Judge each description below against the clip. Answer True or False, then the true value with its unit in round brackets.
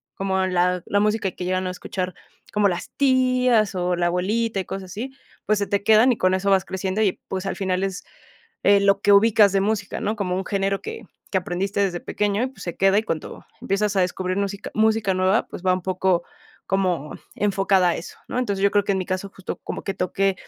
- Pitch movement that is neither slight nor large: False (1.9 semitones)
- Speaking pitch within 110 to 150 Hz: False (195 Hz)